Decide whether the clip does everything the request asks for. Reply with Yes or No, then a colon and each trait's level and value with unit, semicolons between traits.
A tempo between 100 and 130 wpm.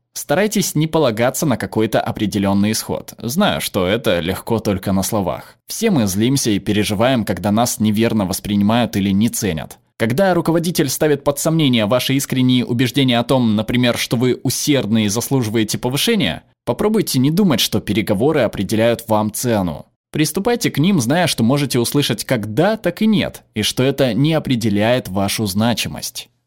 No: fast, 160 wpm